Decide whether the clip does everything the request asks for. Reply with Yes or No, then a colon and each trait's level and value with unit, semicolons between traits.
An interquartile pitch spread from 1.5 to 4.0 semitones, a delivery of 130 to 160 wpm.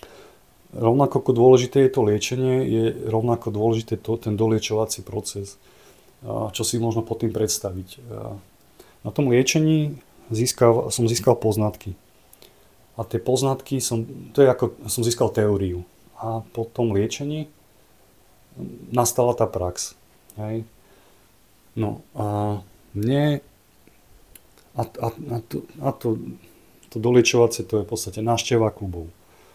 No: average, 2.9 semitones; average, 120 wpm